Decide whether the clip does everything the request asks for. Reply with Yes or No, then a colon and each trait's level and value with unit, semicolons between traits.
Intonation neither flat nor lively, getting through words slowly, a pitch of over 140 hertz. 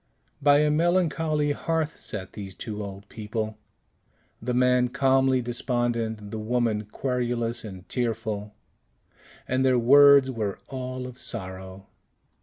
No: average, 3.6 semitones; slow, 120 wpm; low, 120 Hz